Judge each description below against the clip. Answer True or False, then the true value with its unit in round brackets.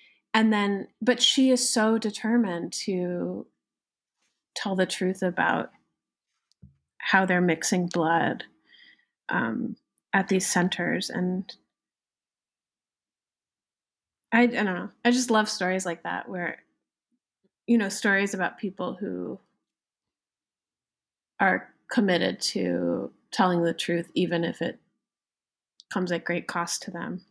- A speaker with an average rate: False (115 wpm)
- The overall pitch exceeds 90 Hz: True (190 Hz)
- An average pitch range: True (3.9 semitones)